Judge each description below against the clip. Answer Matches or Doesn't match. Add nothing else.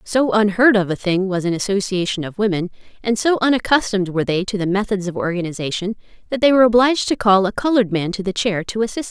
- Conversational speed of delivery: Doesn't match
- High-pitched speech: Matches